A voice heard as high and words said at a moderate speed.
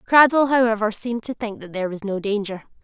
No: high, 220 Hz; fast, 210 wpm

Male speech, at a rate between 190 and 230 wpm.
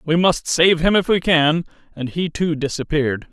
Yes: male; average, 200 wpm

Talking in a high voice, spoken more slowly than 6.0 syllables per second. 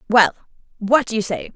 Yes: high, 220 Hz; 5.7 syllables/s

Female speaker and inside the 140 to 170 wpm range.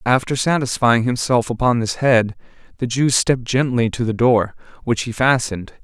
No: male; average, 165 wpm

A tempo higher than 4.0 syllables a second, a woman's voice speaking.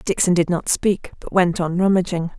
Yes: 5.1 syllables/s; female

